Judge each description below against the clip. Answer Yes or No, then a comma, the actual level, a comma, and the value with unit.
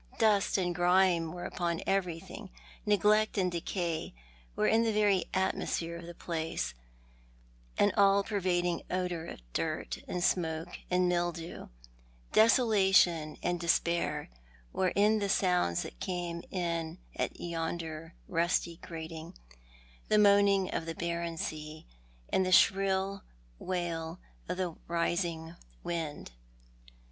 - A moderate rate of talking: No, slow, 120 wpm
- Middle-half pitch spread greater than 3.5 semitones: No, narrow, 2.5 semitones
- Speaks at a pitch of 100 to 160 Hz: No, medium, 175 Hz